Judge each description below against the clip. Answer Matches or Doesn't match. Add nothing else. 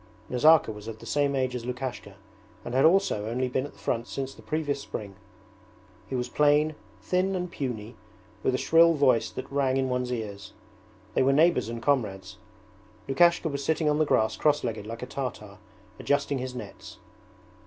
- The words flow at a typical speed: Matches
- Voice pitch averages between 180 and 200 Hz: Doesn't match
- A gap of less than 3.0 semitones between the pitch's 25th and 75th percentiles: Doesn't match